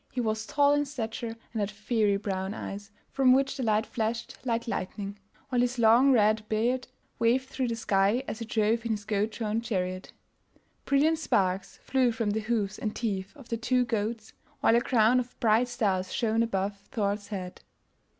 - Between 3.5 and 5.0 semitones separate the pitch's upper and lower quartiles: No, average, 2.8 semitones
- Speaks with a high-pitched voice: Yes, high, 225 Hz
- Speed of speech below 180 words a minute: No, average, 185 wpm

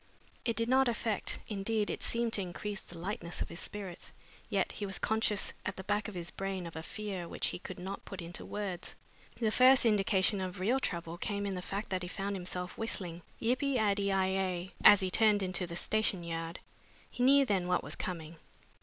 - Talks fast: Yes, fast, 215 wpm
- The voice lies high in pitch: Yes, high, 195 Hz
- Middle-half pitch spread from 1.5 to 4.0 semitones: Yes, average, 3.0 semitones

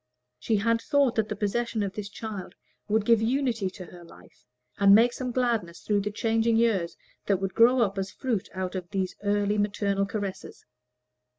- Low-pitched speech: No, high, 210 Hz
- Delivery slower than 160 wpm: No, average, 180 wpm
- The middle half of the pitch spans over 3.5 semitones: No, average, 2.7 semitones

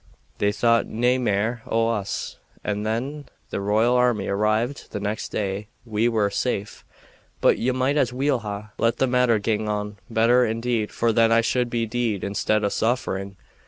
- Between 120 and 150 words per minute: No, average, 175 wpm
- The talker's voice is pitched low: Yes, low, 115 Hz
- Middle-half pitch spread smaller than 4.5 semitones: Yes, average, 2.7 semitones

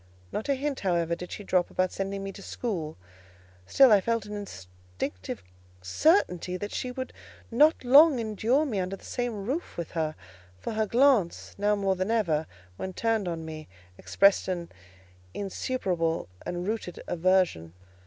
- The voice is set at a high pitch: Yes, high, 195 Hz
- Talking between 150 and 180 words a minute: Yes, average, 160 wpm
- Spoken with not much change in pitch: No, average, 5.1 semitones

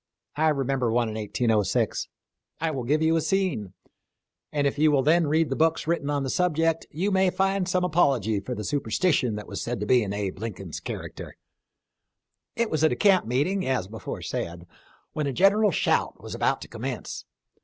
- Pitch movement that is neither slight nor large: No, wide, 6.8 semitones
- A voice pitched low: No, medium, 145 Hz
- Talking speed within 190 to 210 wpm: Yes, average, 195 wpm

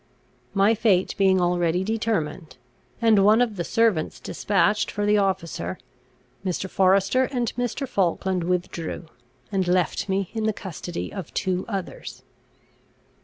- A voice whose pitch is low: No, high, 190 Hz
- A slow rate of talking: Yes, slow, 130 wpm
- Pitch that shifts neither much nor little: Yes, average, 3.2 semitones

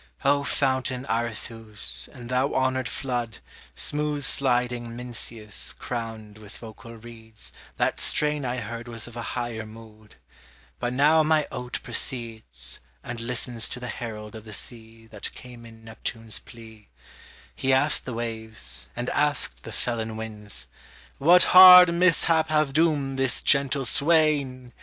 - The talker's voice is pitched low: Yes, low, 120 Hz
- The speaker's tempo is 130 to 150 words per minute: Yes, average, 140 wpm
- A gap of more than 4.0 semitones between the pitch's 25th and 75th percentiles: No, average, 3.3 semitones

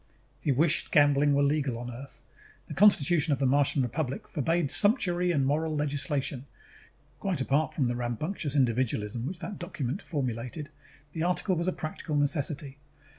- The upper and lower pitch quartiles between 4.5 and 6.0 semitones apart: No, average, 3.7 semitones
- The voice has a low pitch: No, medium, 145 Hz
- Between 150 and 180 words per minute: Yes, average, 160 wpm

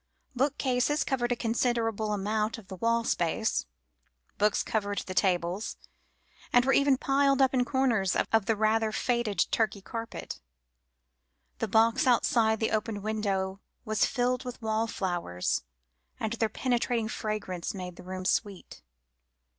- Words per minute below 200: Yes, slow, 135 wpm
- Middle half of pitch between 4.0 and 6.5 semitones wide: No, average, 3.2 semitones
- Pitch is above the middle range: Yes, high, 220 Hz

